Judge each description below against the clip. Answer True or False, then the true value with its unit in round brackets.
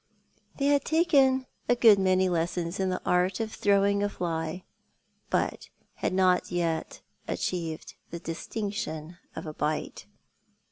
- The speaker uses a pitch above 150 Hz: True (185 Hz)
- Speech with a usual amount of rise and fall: True (3.7 semitones)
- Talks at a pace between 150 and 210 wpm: False (135 wpm)